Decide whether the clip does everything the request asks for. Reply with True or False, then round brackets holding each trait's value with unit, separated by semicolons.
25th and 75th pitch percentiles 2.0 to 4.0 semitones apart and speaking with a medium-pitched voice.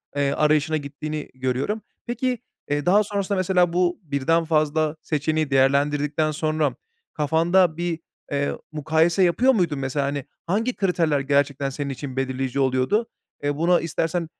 True (3.7 semitones; 155 Hz)